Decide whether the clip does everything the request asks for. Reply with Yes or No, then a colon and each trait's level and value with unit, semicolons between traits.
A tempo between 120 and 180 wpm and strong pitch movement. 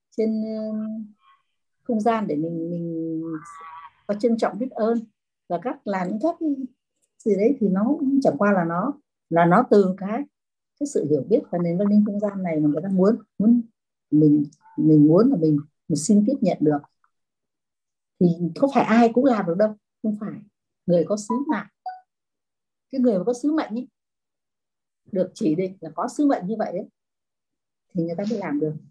No: average, 190 wpm; wide, 6.0 semitones